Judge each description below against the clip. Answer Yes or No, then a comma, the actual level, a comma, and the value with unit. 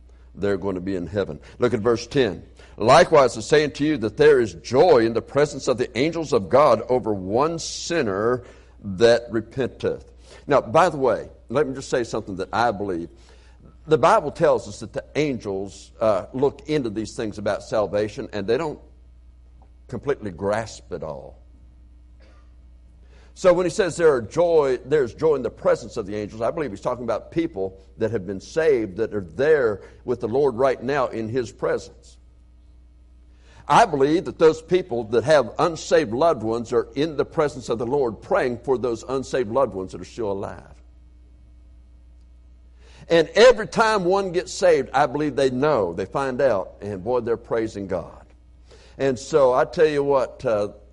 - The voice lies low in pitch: Yes, low, 110 Hz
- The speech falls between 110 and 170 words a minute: No, average, 180 wpm